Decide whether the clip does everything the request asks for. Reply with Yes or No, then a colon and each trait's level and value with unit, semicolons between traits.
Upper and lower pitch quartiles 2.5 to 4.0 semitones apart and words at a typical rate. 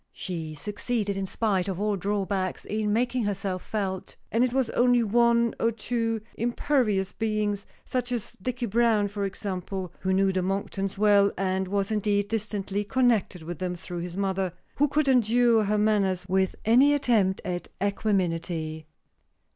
Yes: average, 3.3 semitones; average, 155 wpm